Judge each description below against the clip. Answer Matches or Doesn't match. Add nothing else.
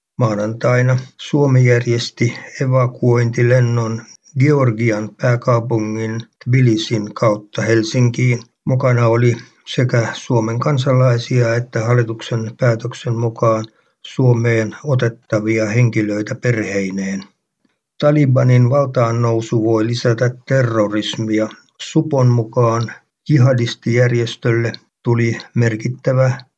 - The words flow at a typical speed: Doesn't match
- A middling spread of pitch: Doesn't match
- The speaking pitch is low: Matches